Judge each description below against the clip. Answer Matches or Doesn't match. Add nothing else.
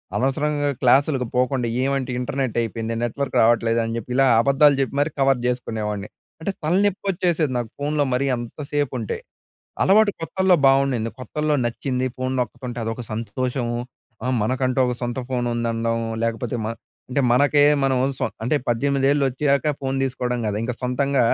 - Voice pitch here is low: Matches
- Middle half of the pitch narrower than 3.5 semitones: Matches